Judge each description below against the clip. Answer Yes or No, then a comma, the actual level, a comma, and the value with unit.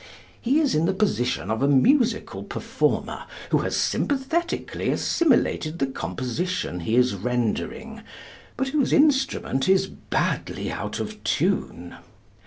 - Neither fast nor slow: No, slow, 125 wpm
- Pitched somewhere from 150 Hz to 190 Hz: Yes, medium, 185 Hz